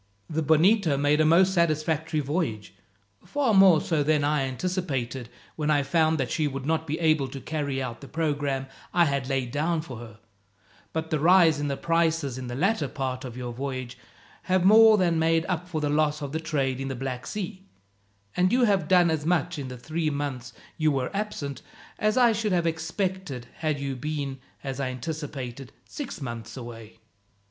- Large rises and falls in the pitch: No, average, 3.9 semitones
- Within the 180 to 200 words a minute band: Yes, average, 190 wpm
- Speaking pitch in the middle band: Yes, medium, 150 Hz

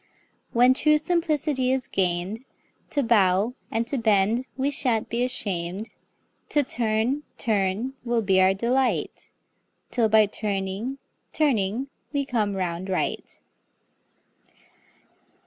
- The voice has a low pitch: No, high, 230 Hz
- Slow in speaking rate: Yes, slow, 110 wpm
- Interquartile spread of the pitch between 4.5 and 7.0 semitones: Yes, average, 5.0 semitones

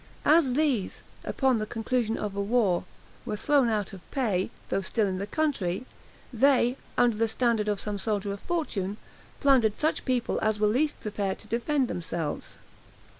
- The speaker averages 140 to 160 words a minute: No, average, 170 wpm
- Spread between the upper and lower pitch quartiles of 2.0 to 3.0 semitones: No, average, 4.2 semitones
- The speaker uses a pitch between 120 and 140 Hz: No, high, 220 Hz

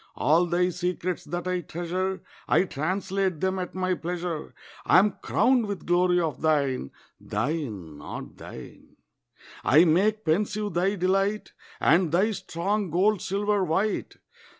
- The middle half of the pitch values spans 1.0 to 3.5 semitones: Yes, average, 3.0 semitones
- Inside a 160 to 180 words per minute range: No, slow, 135 wpm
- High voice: No, medium, 180 Hz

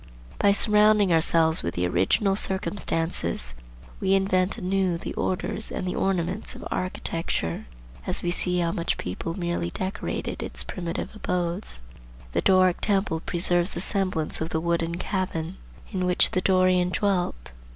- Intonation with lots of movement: No, narrow, 2.5 semitones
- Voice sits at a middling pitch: Yes, medium, 180 Hz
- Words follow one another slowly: No, average, 145 wpm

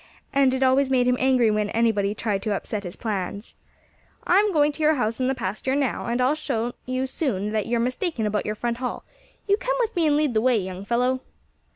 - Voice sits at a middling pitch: No, very high, 250 Hz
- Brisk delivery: Yes, fast, 225 wpm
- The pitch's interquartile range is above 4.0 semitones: Yes, average, 4.4 semitones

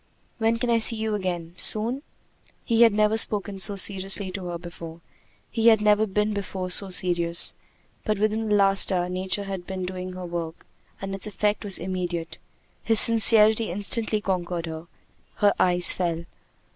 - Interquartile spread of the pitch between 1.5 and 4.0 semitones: Yes, average, 3.1 semitones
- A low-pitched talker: No, high, 195 Hz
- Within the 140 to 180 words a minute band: Yes, average, 170 wpm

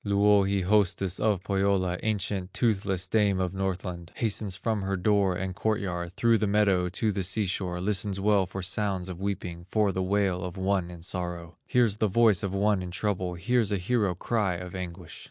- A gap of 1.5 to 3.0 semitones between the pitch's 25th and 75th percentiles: Yes, narrow, 2.4 semitones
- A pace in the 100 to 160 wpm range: No, average, 190 wpm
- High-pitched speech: No, very low, 95 Hz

